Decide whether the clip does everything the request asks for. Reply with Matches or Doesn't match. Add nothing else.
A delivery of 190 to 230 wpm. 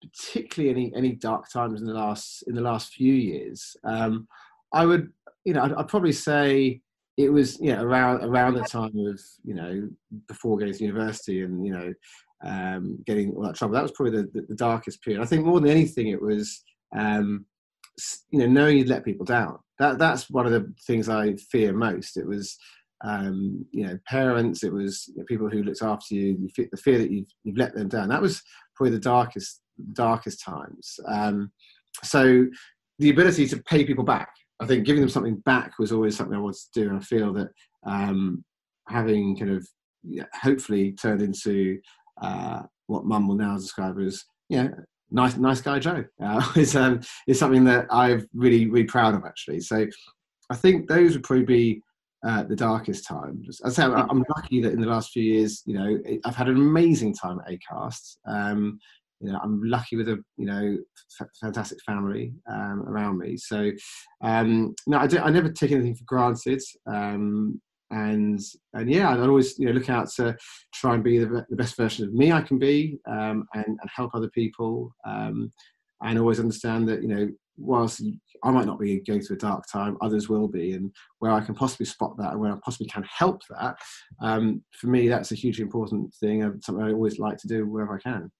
Matches